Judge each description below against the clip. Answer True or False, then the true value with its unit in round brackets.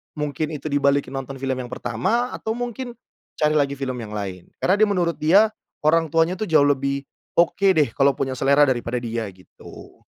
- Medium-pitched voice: True (145 Hz)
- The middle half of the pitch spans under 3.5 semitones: False (4.4 semitones)